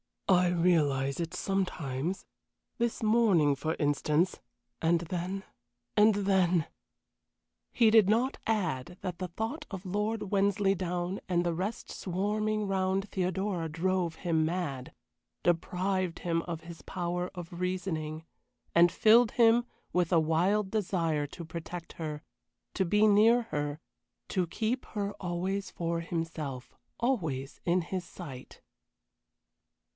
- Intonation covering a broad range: No, average, 3.2 semitones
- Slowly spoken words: Yes, slow, 125 wpm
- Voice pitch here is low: No, medium, 180 Hz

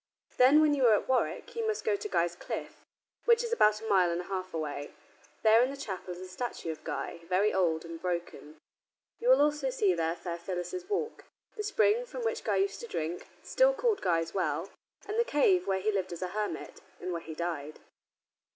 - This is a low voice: No, high, 205 Hz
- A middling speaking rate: No, fast, 215 wpm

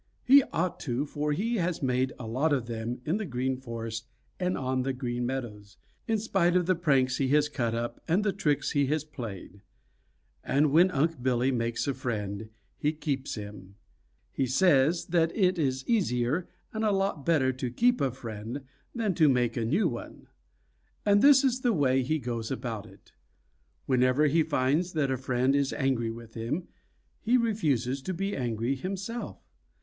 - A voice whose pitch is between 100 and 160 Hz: Yes, low, 135 Hz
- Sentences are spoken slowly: No, average, 180 wpm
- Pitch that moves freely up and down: Yes, wide, 5.9 semitones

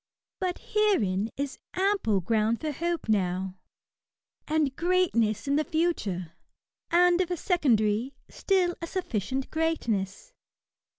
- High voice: Yes, very high, 285 Hz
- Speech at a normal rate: No, slow, 115 wpm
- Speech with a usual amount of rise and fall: No, wide, 8.7 semitones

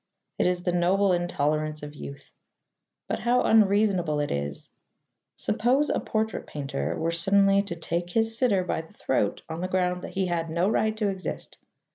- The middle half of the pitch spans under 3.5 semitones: No, average, 3.9 semitones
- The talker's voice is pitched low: No, medium, 180 Hz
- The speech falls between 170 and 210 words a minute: Yes, average, 175 wpm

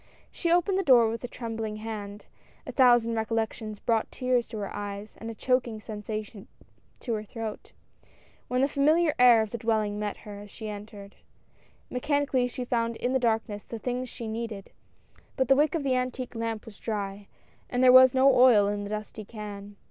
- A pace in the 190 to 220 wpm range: Yes, average, 195 wpm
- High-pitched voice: Yes, high, 225 Hz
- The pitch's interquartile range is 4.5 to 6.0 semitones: No, average, 3.0 semitones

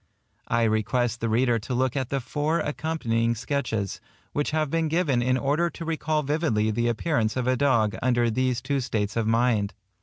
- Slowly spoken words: No, average, 185 wpm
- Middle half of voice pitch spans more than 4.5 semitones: No, average, 4.2 semitones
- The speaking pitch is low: Yes, low, 125 Hz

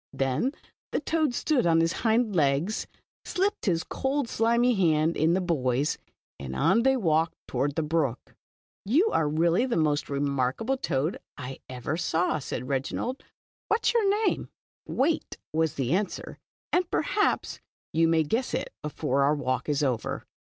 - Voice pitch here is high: No, medium, 165 Hz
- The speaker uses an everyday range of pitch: No, wide, 9.0 semitones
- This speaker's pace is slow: No, average, 170 wpm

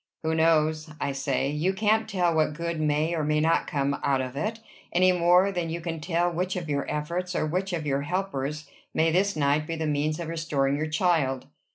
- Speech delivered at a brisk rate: Yes, fast, 215 wpm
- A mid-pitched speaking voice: Yes, medium, 160 Hz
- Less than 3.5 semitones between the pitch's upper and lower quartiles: Yes, average, 2.8 semitones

